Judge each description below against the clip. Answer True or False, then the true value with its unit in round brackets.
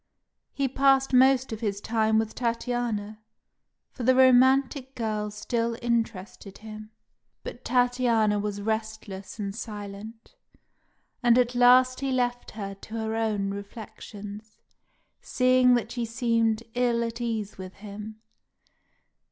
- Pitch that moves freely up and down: False (2.7 semitones)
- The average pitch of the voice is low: False (230 Hz)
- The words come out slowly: True (125 wpm)